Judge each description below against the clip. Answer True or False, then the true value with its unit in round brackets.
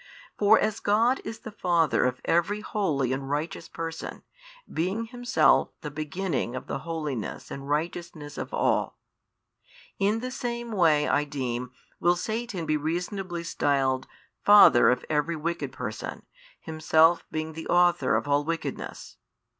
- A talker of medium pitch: True (165 Hz)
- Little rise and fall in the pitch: False (5.3 semitones)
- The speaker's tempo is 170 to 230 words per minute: False (140 wpm)